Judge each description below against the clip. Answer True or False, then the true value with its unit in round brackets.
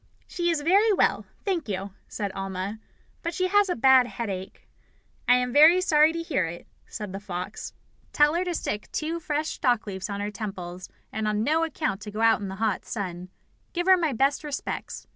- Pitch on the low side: False (240 Hz)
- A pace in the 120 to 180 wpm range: False (200 wpm)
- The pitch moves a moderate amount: False (8.3 semitones)